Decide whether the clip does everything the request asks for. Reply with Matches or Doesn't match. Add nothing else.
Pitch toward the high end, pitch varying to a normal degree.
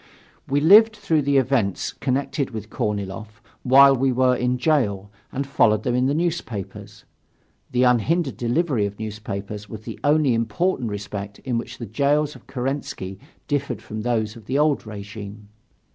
Doesn't match